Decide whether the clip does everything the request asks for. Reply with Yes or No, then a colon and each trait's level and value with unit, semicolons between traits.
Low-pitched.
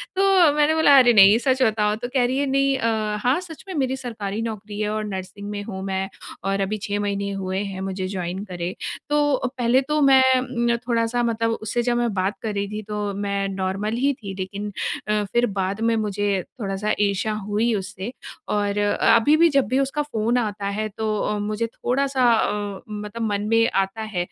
No: high, 215 Hz